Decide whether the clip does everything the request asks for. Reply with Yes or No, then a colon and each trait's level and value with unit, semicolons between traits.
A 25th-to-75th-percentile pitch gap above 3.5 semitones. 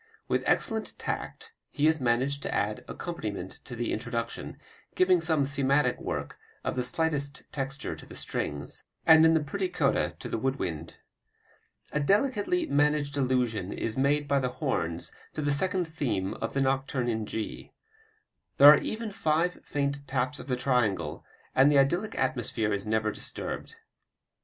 Yes: average, 4.8 semitones